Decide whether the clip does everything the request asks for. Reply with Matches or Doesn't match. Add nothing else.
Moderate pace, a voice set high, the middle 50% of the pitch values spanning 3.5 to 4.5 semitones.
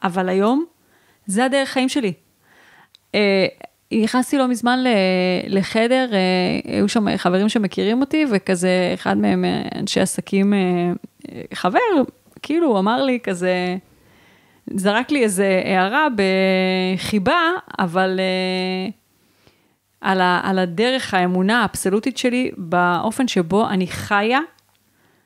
Doesn't match